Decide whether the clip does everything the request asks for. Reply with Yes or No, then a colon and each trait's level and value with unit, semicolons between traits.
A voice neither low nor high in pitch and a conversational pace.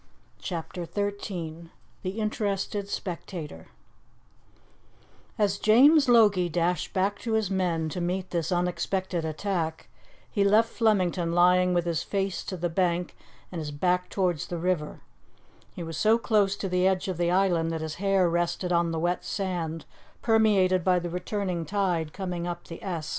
Yes: medium, 180 Hz; average, 160 wpm